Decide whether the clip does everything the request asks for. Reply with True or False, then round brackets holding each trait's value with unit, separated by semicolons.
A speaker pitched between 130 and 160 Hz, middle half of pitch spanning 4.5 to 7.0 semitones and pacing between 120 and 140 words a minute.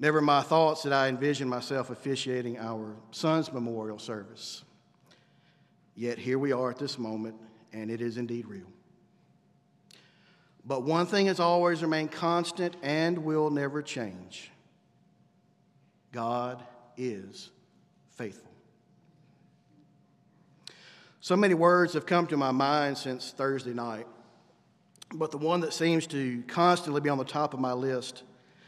True (135 Hz; 4.8 semitones; 135 wpm)